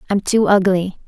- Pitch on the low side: No, high, 190 Hz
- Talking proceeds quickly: Yes, fast, 225 wpm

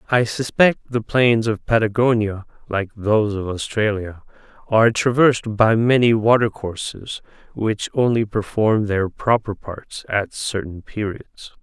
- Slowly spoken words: Yes, slow, 130 wpm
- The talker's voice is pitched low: Yes, low, 110 Hz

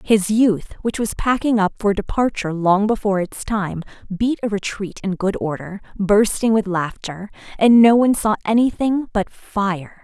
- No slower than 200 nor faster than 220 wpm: No, average, 165 wpm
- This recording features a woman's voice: Yes, female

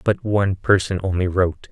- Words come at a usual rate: Yes, average, 175 wpm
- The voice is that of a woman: No, male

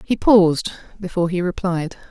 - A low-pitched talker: No, medium, 185 Hz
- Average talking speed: Yes, average, 145 wpm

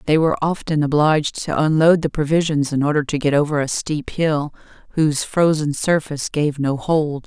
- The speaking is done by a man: No, female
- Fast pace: No, average, 180 wpm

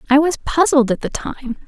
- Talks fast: Yes, fast, 215 wpm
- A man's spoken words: No, female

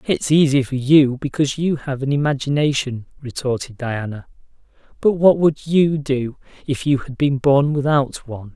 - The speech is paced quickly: No, average, 160 wpm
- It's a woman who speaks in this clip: No, male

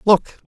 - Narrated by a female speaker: Yes, female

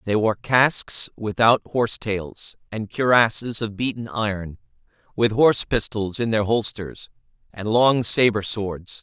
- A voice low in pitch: Yes, low, 110 Hz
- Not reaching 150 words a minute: Yes, average, 140 wpm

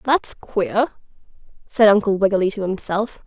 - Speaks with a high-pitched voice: Yes, high, 210 Hz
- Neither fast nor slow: No, slow, 130 wpm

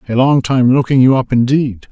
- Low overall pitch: Yes, low, 130 Hz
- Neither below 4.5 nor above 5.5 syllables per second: Yes, 5.2 syllables/s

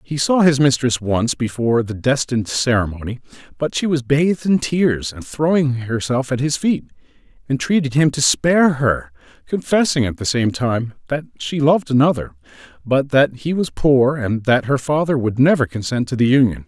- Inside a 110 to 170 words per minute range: No, average, 180 wpm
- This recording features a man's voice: Yes, male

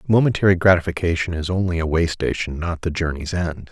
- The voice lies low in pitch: Yes, very low, 85 Hz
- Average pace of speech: Yes, average, 180 wpm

